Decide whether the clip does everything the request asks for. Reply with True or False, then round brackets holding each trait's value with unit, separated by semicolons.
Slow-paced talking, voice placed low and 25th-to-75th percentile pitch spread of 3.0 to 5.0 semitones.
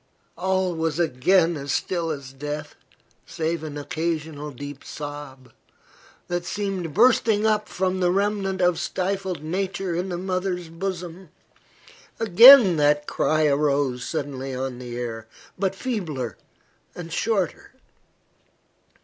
False (115 wpm; 170 Hz; 4.5 semitones)